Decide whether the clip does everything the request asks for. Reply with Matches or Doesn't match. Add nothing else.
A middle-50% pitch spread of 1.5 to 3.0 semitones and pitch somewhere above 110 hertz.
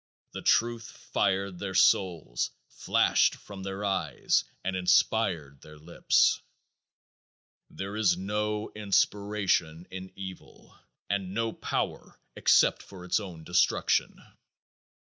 Doesn't match